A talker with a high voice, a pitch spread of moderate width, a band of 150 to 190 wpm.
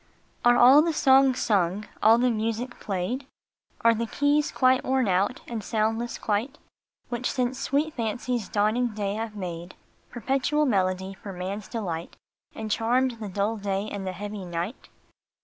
Yes: high, 225 Hz; average, 4.1 semitones; average, 165 wpm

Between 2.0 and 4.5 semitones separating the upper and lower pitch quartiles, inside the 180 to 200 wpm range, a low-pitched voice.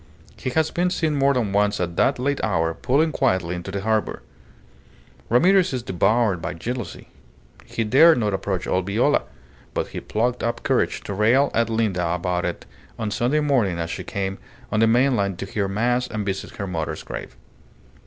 No: average, 4.9 semitones; average, 185 wpm; low, 110 Hz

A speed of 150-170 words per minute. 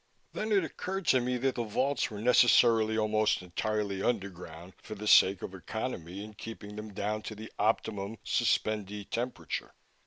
Yes: average, 160 wpm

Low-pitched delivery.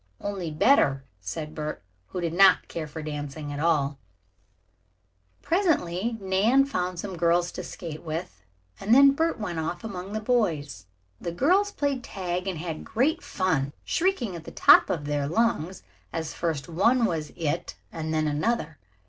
No: medium, 175 Hz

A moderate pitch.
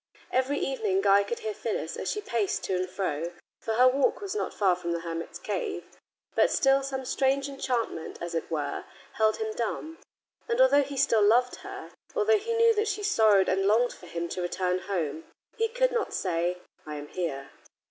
No: high, 220 Hz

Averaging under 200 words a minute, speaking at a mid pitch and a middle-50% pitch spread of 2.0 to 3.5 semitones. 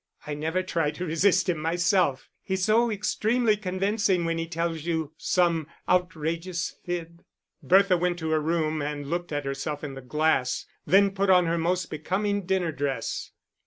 Yes: average, 165 wpm; medium, 170 Hz; average, 3.1 semitones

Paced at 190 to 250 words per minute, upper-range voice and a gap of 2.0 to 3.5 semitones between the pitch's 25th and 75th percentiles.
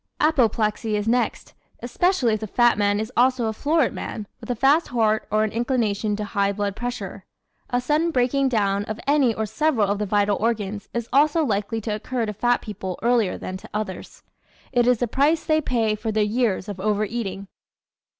Yes: average, 200 wpm; high, 220 Hz; average, 3.2 semitones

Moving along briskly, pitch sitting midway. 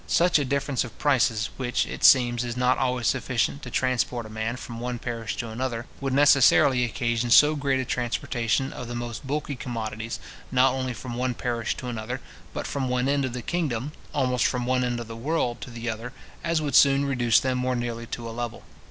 No: fast, 215 wpm; low, 125 Hz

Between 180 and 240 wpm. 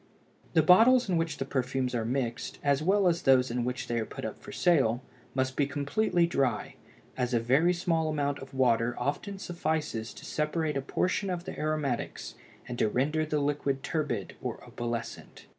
Yes: average, 185 wpm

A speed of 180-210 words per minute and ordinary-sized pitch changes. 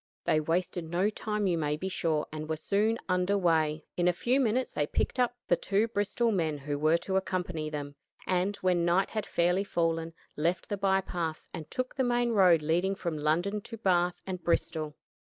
Yes: fast, 205 wpm; average, 3.8 semitones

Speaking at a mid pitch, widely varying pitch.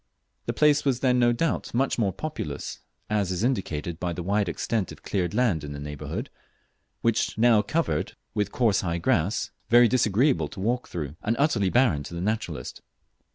No: low, 105 Hz; wide, 6.1 semitones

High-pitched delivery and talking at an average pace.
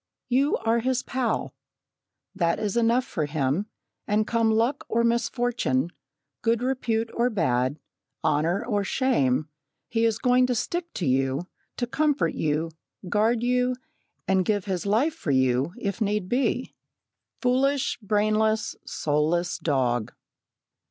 No: high, 215 Hz; slow, 130 wpm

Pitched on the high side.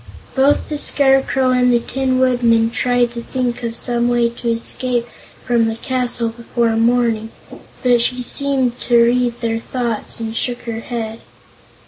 Yes: high, 240 Hz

